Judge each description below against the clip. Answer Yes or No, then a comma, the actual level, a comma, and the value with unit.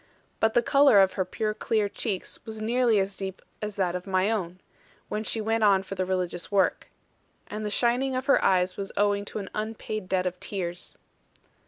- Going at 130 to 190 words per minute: No, average, 200 wpm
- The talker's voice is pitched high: Yes, high, 205 Hz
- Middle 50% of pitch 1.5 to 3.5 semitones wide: Yes, average, 2.8 semitones